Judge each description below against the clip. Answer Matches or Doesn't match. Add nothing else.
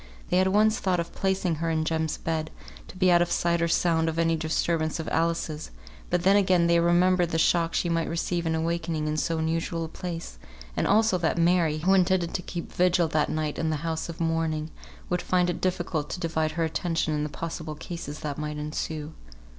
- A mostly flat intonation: Matches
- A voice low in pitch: Doesn't match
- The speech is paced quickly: Matches